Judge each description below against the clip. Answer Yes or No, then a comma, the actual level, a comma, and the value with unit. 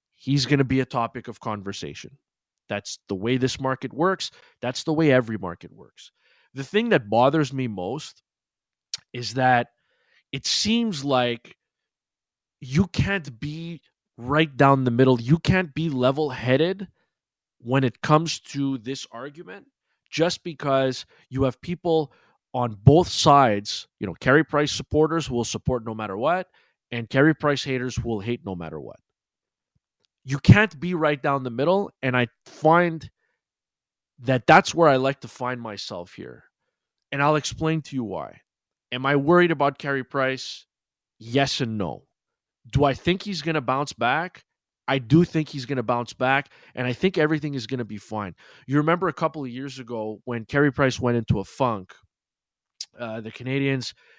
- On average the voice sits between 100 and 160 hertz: Yes, low, 135 Hz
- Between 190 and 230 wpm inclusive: No, average, 165 wpm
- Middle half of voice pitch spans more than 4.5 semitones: No, average, 4.0 semitones